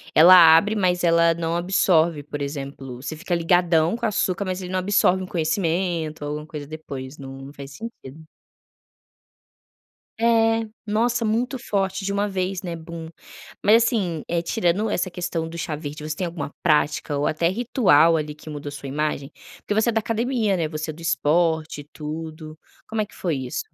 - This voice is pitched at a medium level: Yes, medium, 170 Hz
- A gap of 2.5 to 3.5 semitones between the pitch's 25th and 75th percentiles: No, average, 4.1 semitones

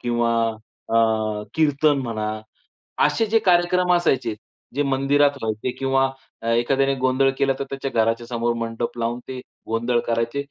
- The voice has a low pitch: Yes, low, 130 Hz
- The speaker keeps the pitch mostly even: No, average, 3.1 semitones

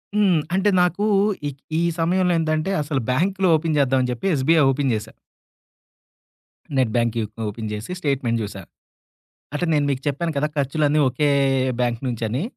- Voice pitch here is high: No, medium, 145 Hz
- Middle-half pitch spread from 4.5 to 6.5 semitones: Yes, average, 5.1 semitones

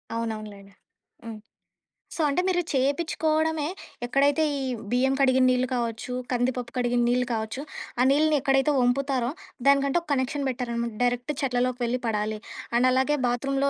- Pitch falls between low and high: No, very high, 255 Hz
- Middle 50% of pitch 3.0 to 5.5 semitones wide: No, narrow, 2.5 semitones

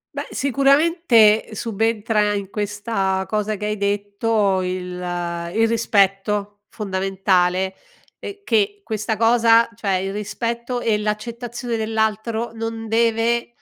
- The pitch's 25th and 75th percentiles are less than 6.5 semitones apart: Yes, narrow, 2.5 semitones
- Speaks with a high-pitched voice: Yes, high, 215 Hz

